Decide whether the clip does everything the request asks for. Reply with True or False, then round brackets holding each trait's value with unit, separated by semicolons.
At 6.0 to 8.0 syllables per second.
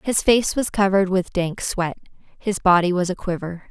False (5.0 syllables/s)